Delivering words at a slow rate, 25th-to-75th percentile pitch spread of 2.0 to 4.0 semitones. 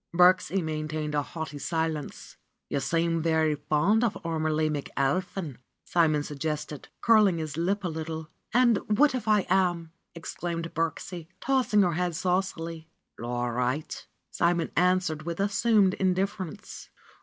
Yes: slow, 130 wpm; average, 3.3 semitones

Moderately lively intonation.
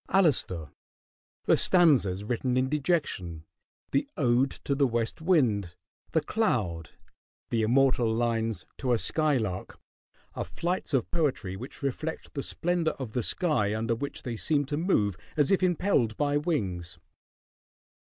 No: wide, 6.1 semitones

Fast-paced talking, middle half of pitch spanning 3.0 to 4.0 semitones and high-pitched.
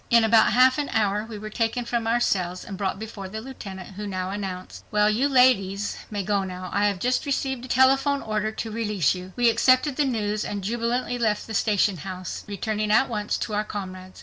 Yes: fast, 210 wpm; average, 3.3 semitones; high, 215 Hz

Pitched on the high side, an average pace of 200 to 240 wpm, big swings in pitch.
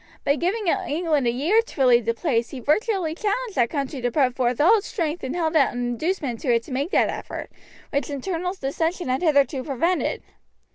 Yes: very high, 295 Hz; fast, 205 wpm; wide, 5.8 semitones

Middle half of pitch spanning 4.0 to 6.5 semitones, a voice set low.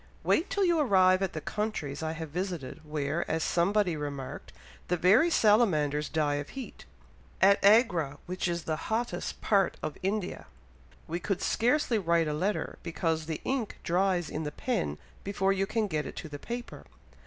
No: average, 5.1 semitones; medium, 180 Hz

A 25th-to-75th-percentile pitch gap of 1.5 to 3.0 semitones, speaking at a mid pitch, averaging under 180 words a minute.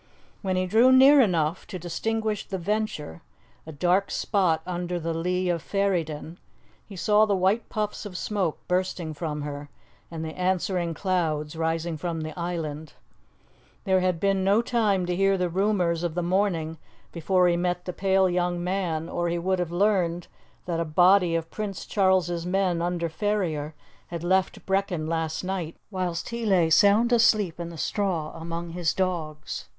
Yes: average, 2.7 semitones; medium, 180 Hz; average, 170 wpm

